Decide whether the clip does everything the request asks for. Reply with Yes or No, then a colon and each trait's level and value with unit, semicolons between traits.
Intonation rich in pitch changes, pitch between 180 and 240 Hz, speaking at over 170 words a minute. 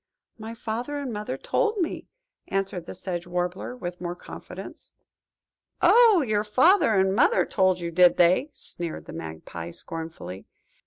No: wide, 6.4 semitones; high, 190 Hz; average, 150 wpm